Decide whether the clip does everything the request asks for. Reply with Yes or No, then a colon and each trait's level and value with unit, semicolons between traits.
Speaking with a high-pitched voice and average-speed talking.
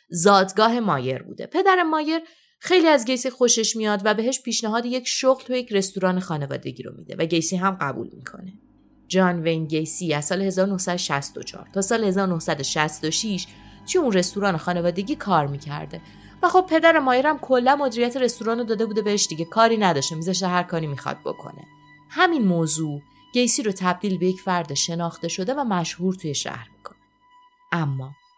No: high, 195 Hz; fast, 165 wpm